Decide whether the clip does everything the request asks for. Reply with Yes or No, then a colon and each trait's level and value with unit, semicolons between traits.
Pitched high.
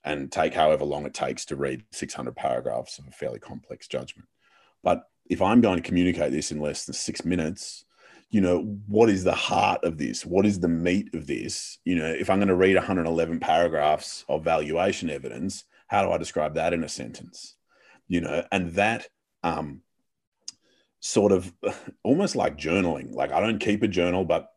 No: very low, 90 Hz